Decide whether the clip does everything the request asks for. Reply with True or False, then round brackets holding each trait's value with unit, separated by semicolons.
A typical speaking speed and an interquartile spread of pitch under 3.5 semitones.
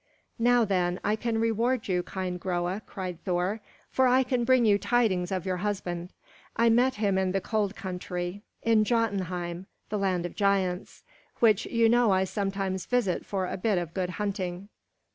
False (175 wpm; 3.8 semitones)